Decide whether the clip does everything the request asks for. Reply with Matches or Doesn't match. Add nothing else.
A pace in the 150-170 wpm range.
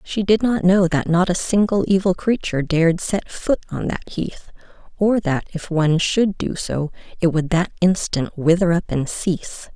Doesn't match